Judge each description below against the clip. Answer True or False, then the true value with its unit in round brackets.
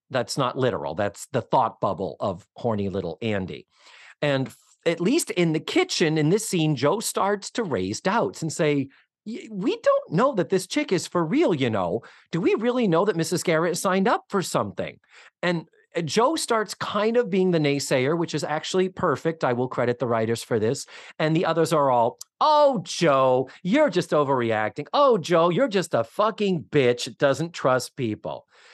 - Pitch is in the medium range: True (165 Hz)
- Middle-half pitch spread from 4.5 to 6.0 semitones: True (5.5 semitones)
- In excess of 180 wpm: True (190 wpm)